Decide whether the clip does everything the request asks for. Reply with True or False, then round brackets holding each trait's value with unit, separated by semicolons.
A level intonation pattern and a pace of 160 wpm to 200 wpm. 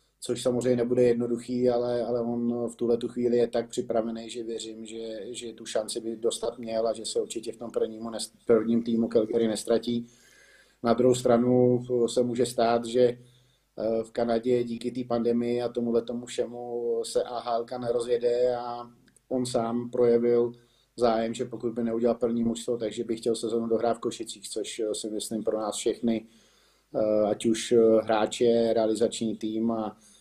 True (1.1 semitones; 165 wpm)